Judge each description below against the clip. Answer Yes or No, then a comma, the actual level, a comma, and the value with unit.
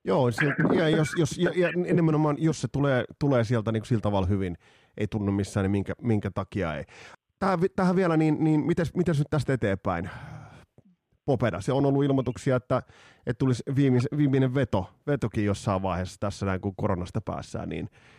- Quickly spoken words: Yes, fast, 185 wpm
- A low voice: Yes, low, 125 Hz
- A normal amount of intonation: No, wide, 6.9 semitones